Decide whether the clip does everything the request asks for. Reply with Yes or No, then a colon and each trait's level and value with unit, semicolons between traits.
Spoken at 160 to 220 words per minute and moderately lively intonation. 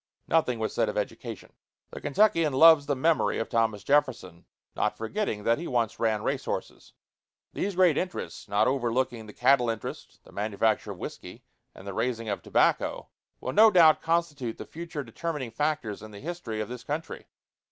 No: average, 175 wpm; wide, 6.4 semitones